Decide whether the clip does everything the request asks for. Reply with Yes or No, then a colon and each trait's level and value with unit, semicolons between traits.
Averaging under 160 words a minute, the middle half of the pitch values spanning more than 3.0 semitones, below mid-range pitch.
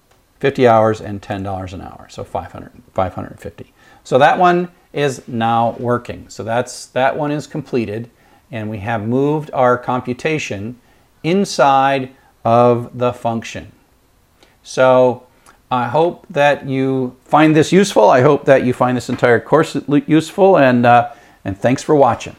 Yes: average, 145 wpm; average, 3.5 semitones; low, 125 Hz